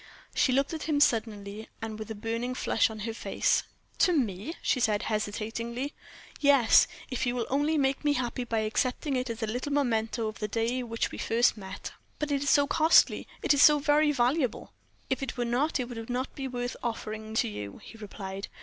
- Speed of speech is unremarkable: No, fast, 210 wpm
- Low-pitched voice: No, high, 240 Hz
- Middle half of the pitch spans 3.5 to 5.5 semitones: Yes, average, 4.0 semitones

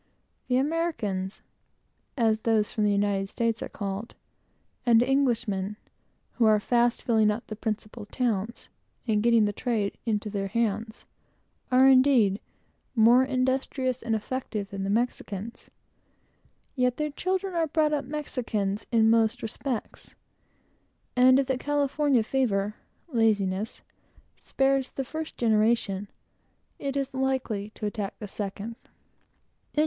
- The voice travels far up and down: No, average, 3.8 semitones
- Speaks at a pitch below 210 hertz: No, high, 230 Hz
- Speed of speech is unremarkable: No, slow, 125 wpm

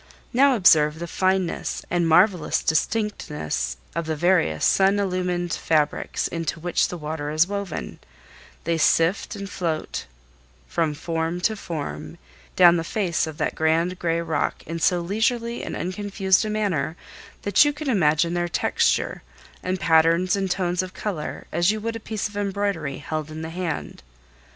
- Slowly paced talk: No, average, 160 wpm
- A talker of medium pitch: Yes, medium, 175 Hz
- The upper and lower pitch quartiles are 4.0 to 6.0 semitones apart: No, average, 3.6 semitones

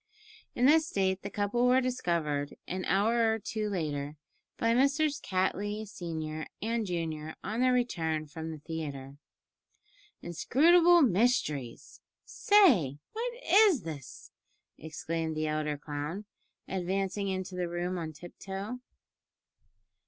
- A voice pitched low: No, high, 190 Hz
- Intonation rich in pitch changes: Yes, wide, 6.8 semitones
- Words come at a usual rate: No, slow, 120 wpm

